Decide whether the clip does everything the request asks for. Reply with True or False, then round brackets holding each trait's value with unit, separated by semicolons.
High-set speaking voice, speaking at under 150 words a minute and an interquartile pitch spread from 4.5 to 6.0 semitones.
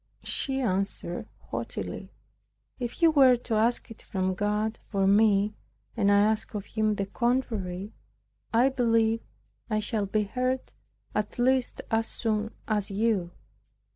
False (220 Hz; 140 wpm; 2.8 semitones)